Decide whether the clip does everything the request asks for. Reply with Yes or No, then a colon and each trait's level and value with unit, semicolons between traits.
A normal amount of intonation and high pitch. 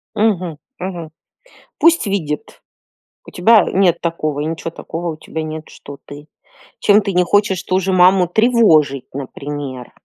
No: average, 4.2 semitones; medium, 175 Hz